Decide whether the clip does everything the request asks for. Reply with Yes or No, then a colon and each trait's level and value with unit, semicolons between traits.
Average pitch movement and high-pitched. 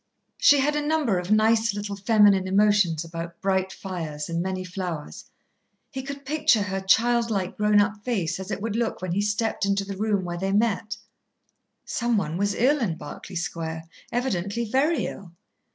Yes: average, 3.6 semitones; high, 200 Hz